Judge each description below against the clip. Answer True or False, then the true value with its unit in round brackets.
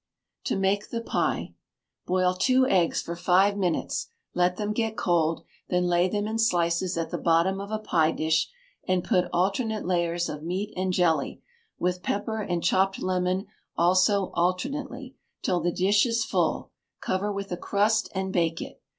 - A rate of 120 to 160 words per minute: False (170 wpm)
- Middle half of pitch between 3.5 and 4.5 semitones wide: False (2.9 semitones)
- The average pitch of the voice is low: False (185 Hz)